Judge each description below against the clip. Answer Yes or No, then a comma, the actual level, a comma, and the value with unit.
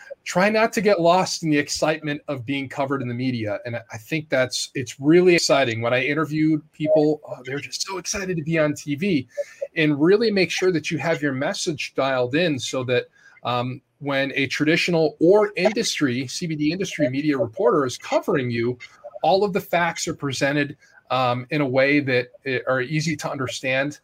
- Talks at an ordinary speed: Yes, average, 185 wpm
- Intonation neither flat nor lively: Yes, average, 4.3 semitones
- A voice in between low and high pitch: Yes, medium, 150 Hz